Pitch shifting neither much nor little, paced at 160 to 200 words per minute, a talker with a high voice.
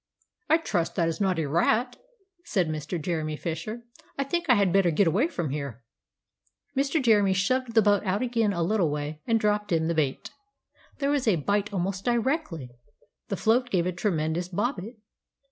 No: wide, 6.0 semitones; average, 180 wpm; high, 195 Hz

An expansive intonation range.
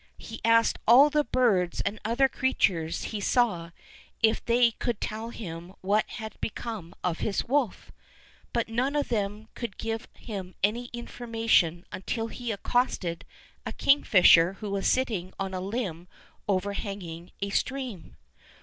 No: average, 4.1 semitones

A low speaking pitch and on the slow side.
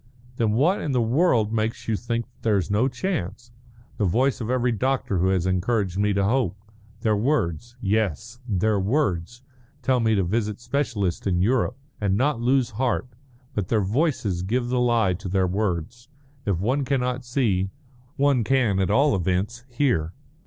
No: low, 115 Hz; average, 170 wpm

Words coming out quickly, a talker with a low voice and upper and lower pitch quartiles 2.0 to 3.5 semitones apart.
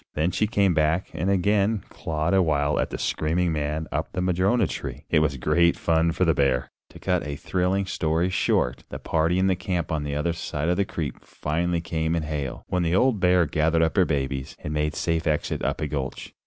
Yes: fast, 220 wpm; very low, 80 Hz; average, 3.1 semitones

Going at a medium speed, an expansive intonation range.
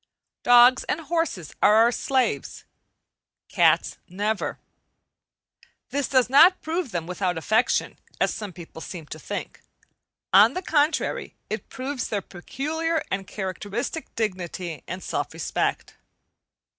No: slow, 120 wpm; wide, 7.4 semitones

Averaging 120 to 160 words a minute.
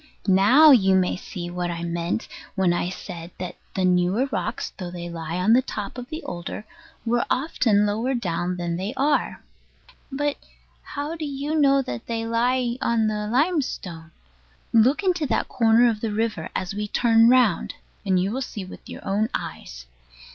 No: average, 175 wpm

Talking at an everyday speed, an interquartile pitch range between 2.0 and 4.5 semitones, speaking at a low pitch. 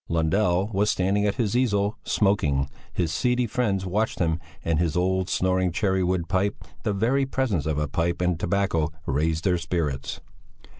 Yes: average, 165 wpm; average, 3.7 semitones; very low, 95 Hz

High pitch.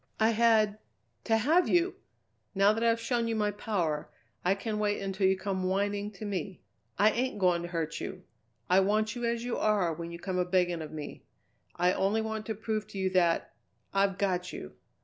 Yes: high, 200 Hz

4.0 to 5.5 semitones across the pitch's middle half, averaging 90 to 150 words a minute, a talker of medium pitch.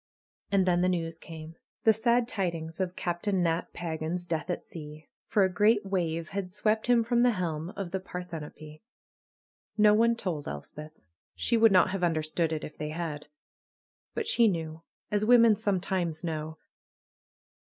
No: average, 4.5 semitones; average, 165 wpm; medium, 180 Hz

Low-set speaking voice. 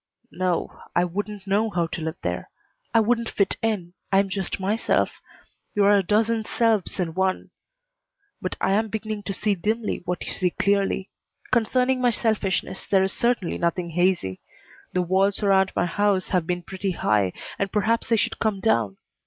No: high, 195 Hz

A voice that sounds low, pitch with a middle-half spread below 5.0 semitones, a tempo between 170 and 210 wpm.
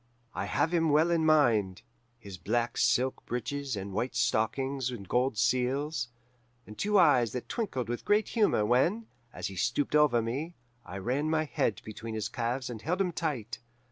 No: low, 125 Hz; average, 5.3 semitones; average, 175 wpm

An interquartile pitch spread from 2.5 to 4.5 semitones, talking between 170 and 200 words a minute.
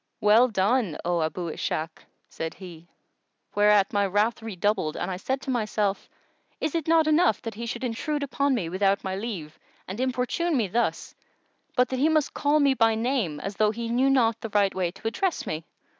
No: average, 5.2 semitones; average, 190 wpm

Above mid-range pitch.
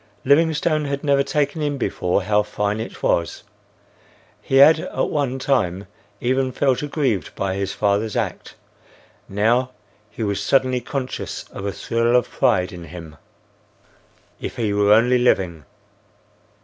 No: low, 120 Hz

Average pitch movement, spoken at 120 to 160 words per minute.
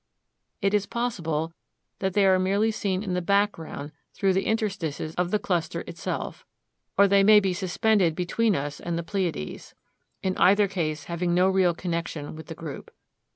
No: average, 3.1 semitones; average, 170 wpm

